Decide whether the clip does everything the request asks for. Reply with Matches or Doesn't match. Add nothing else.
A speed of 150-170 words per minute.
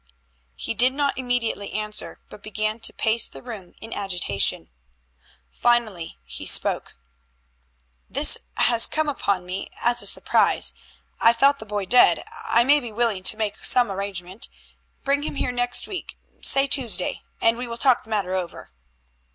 Matches